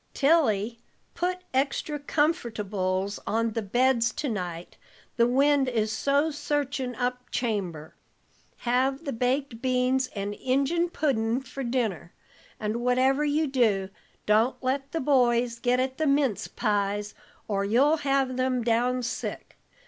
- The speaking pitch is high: Yes, very high, 250 Hz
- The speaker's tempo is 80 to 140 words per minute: Yes, slow, 135 wpm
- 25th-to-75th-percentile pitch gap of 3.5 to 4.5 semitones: Yes, average, 3.8 semitones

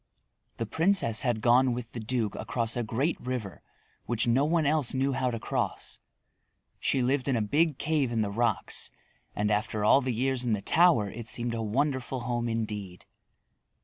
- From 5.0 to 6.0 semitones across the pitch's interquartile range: No, average, 3.2 semitones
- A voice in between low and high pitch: No, low, 120 Hz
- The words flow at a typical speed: Yes, average, 180 wpm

